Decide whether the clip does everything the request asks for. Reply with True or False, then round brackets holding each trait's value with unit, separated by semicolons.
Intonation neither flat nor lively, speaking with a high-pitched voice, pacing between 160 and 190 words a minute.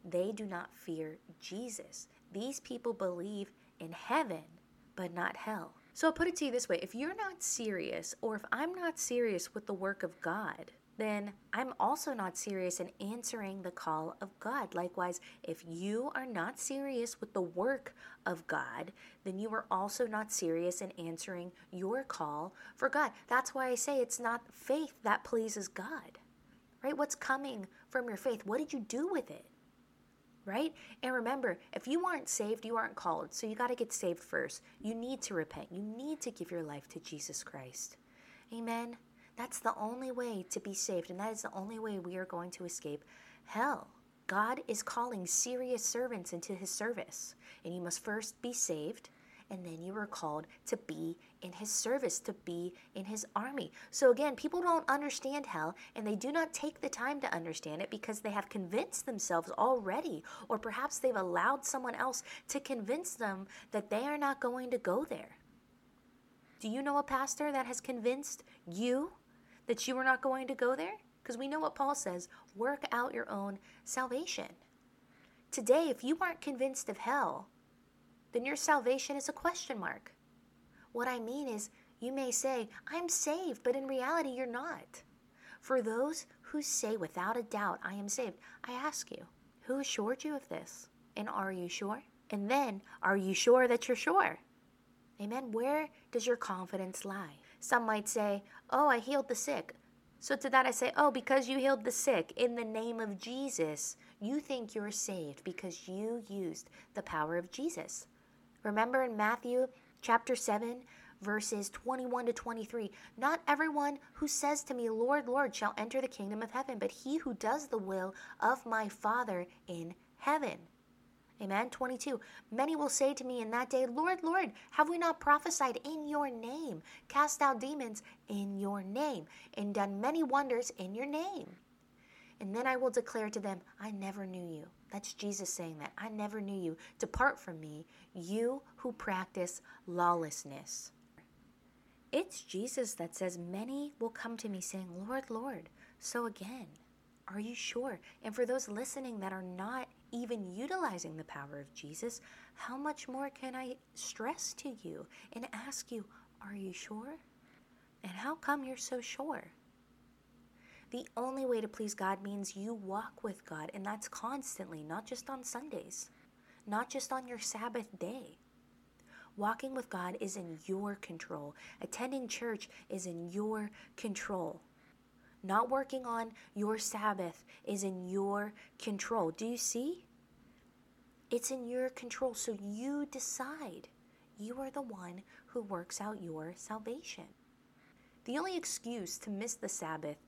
True (5.0 semitones; 235 Hz; 175 wpm)